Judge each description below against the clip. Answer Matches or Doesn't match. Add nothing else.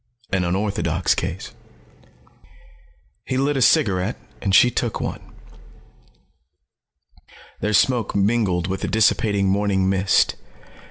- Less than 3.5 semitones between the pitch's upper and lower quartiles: Matches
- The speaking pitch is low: Matches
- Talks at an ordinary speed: Doesn't match